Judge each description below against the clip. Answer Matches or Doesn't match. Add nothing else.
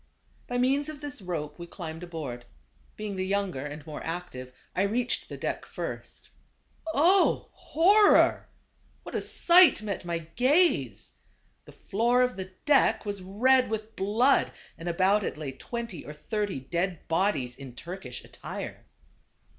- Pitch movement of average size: Doesn't match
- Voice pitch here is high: Matches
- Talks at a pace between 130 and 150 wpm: Matches